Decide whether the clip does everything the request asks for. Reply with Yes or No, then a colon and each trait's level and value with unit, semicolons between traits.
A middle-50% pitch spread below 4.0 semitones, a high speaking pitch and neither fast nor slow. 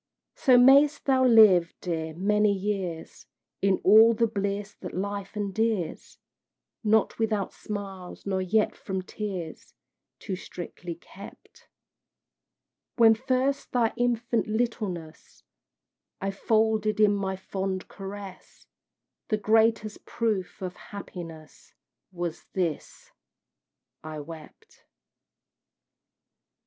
No: average, 3.2 semitones; high, 200 Hz; slow, 100 wpm